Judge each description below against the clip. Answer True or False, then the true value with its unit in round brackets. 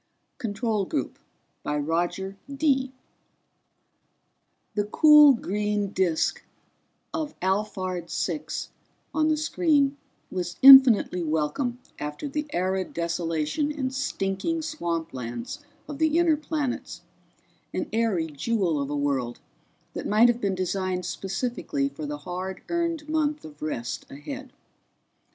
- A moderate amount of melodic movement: False (8.9 semitones)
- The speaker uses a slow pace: True (120 wpm)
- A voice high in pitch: True (205 Hz)